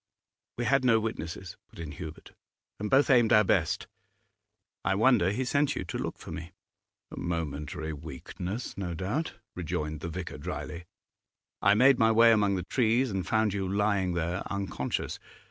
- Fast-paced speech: No, average, 165 wpm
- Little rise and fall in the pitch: No, average, 5.0 semitones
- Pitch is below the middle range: Yes, very low, 95 Hz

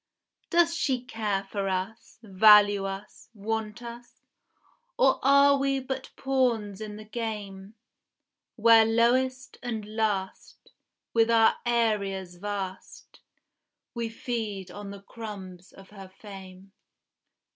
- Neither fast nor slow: No, slow, 115 wpm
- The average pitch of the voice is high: Yes, high, 215 Hz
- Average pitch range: Yes, average, 3.2 semitones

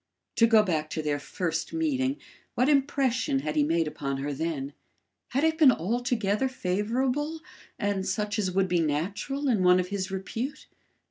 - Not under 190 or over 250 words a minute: No, average, 170 wpm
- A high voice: Yes, high, 205 Hz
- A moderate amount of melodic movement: No, wide, 7.8 semitones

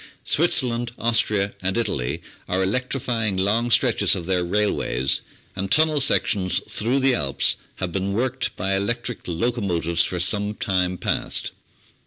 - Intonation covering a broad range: No, average, 4.4 semitones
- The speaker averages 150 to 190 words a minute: No, average, 140 wpm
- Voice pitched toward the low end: Yes, low, 100 Hz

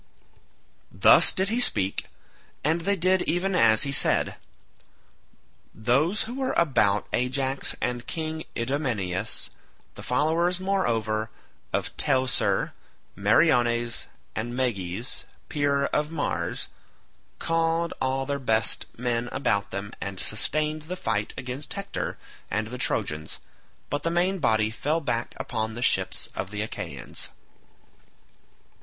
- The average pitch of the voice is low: Yes, low, 130 Hz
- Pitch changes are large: Yes, wide, 6.7 semitones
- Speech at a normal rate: No, slow, 125 wpm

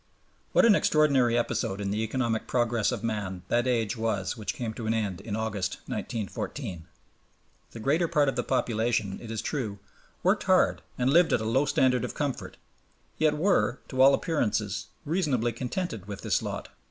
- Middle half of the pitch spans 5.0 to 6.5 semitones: No, average, 4.0 semitones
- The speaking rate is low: No, average, 175 wpm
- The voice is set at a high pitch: No, low, 115 Hz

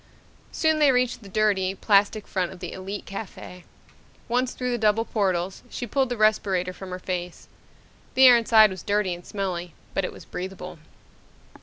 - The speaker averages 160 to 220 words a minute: Yes, average, 175 wpm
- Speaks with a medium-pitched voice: No, high, 200 Hz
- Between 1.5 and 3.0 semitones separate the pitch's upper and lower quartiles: No, average, 3.6 semitones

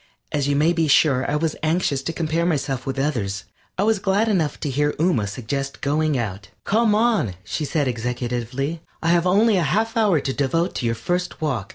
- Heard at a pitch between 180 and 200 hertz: No, medium, 150 Hz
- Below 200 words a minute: No, fast, 205 wpm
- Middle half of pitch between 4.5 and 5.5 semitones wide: Yes, average, 5.2 semitones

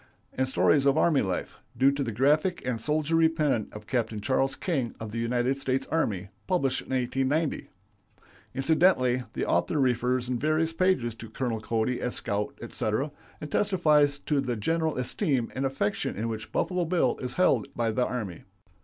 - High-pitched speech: No, low, 130 Hz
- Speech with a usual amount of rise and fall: Yes, average, 4.7 semitones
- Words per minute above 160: Yes, average, 170 wpm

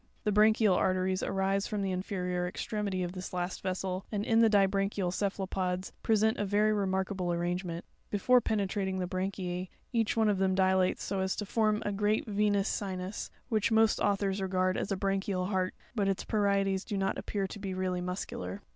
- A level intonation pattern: Yes, narrow, 1.9 semitones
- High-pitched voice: Yes, high, 195 Hz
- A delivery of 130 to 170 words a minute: No, average, 200 wpm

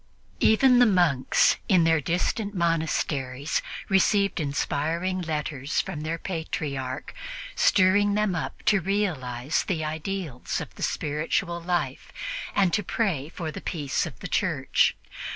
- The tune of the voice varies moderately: Yes, average, 4.5 semitones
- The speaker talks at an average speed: No, slow, 130 wpm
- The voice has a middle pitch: Yes, medium, 165 Hz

